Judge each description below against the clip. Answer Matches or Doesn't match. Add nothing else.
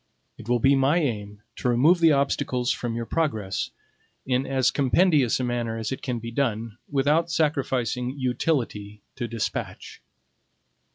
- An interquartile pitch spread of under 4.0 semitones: Matches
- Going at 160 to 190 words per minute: Doesn't match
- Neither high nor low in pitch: Doesn't match